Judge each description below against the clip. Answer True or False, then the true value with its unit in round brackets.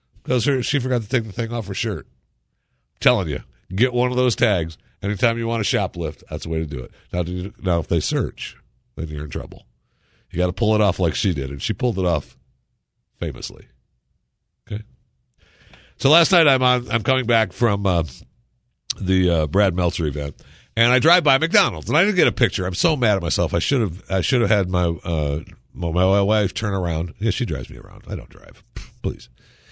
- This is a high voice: False (100 Hz)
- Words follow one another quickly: True (220 wpm)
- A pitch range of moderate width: False (6.0 semitones)